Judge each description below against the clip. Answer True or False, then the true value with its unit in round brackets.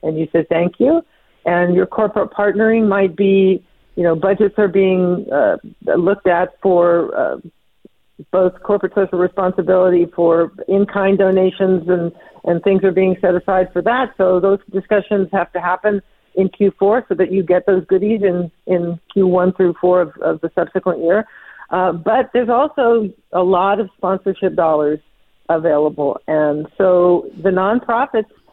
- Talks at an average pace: True (160 wpm)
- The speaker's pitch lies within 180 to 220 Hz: True (190 Hz)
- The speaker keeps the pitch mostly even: True (2.1 semitones)